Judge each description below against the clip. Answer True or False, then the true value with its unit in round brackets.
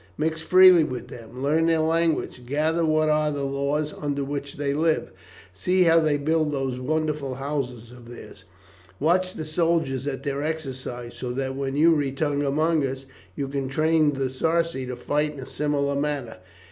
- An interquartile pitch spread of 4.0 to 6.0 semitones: False (2.8 semitones)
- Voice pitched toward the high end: False (145 Hz)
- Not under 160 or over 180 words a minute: True (175 wpm)